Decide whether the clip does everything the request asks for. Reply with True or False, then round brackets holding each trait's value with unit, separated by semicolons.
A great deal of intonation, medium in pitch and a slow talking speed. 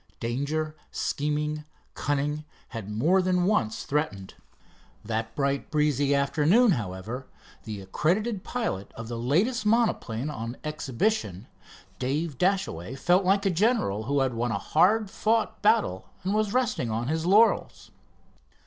True (8.7 semitones; 150 Hz; 130 wpm)